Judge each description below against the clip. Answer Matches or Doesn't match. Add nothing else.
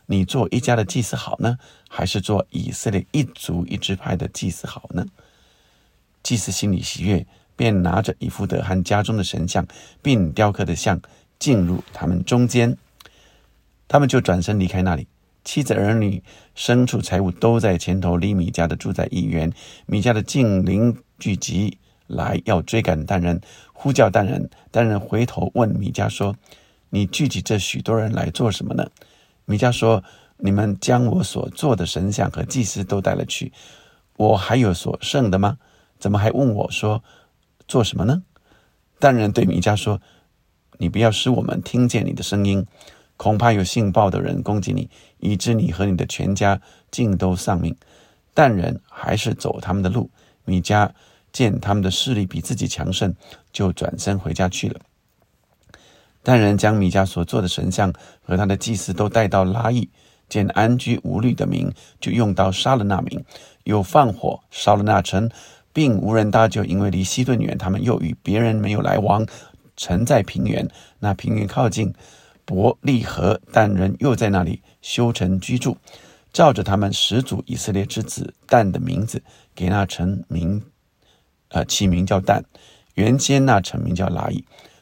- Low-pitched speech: Matches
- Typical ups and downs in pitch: Matches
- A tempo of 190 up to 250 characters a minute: Matches